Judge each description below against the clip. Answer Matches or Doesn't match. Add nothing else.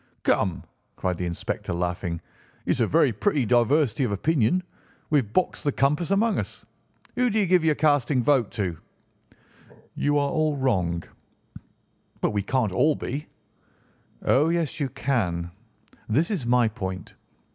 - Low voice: Matches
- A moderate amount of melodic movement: Doesn't match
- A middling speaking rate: Matches